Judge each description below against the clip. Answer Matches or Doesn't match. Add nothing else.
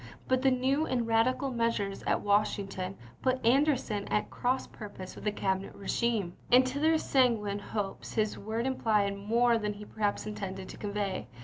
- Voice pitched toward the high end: Matches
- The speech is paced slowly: Doesn't match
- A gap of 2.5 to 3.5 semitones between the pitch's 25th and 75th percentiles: Doesn't match